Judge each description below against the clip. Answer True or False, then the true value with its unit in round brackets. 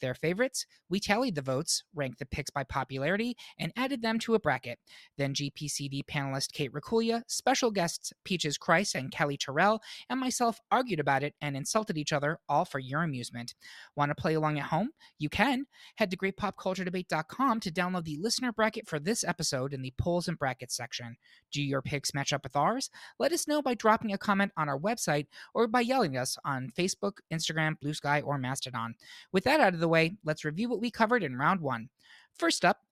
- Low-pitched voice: False (165 Hz)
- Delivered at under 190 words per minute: False (200 wpm)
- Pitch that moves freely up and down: True (7.6 semitones)